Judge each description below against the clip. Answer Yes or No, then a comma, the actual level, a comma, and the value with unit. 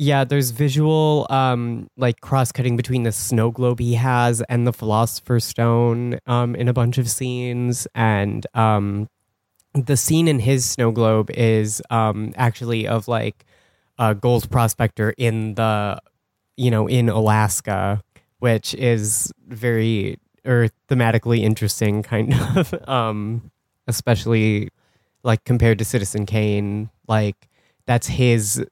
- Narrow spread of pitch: Yes, narrow, 2.3 semitones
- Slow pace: Yes, slow, 130 wpm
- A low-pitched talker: Yes, low, 115 Hz